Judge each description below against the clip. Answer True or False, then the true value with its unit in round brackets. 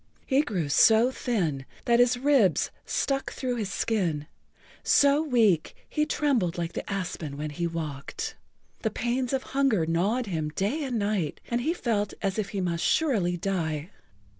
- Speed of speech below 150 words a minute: False (165 wpm)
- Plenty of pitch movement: True (6.9 semitones)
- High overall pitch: True (210 Hz)